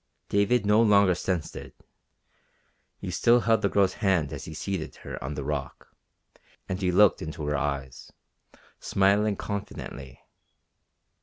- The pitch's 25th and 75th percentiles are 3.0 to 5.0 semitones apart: No, wide, 5.5 semitones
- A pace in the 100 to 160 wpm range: Yes, average, 140 wpm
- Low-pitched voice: Yes, very low, 95 Hz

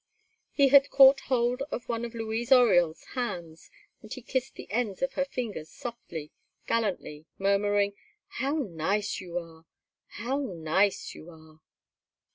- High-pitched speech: Yes, high, 215 Hz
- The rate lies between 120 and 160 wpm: Yes, average, 140 wpm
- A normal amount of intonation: No, wide, 6.5 semitones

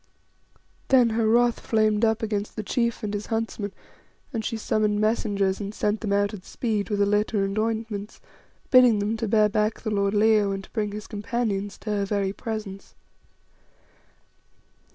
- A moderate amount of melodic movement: No, narrow, 1.6 semitones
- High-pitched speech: Yes, high, 215 Hz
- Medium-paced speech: Yes, average, 175 wpm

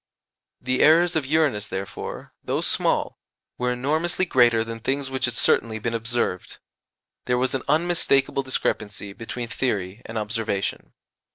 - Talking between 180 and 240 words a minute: No, average, 140 wpm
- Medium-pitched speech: No, low, 125 Hz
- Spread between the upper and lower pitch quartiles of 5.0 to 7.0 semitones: No, average, 3.6 semitones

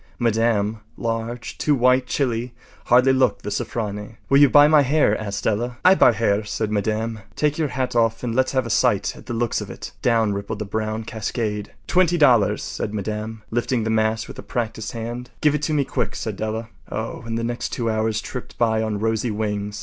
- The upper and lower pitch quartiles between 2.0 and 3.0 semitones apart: Yes, narrow, 2.5 semitones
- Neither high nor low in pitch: No, low, 115 Hz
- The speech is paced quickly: Yes, fast, 210 wpm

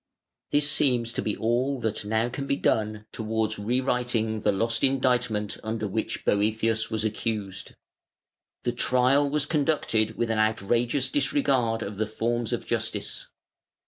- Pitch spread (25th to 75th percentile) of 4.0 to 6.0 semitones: No, average, 2.7 semitones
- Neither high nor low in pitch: No, low, 115 Hz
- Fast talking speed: No, average, 145 wpm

